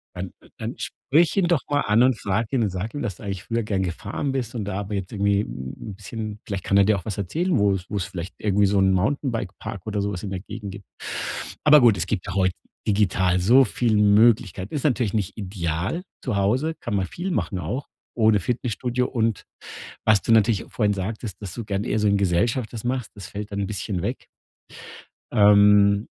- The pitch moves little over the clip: No, average, 3.0 semitones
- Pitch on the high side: No, low, 105 Hz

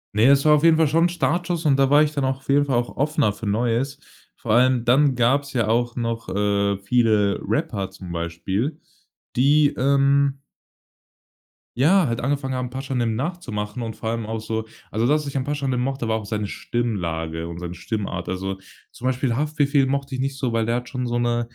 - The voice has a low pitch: Yes, low, 125 Hz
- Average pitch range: Yes, average, 4.2 semitones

